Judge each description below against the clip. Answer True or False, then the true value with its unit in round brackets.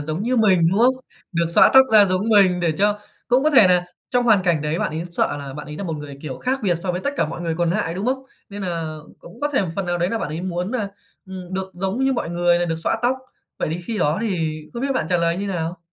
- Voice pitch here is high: False (180 Hz)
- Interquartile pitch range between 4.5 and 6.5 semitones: False (4.1 semitones)